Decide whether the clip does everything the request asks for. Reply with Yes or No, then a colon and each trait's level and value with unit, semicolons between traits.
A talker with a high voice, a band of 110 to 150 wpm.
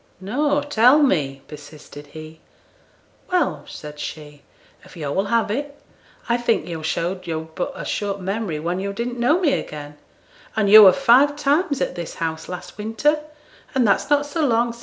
No: high, 210 Hz; average, 180 wpm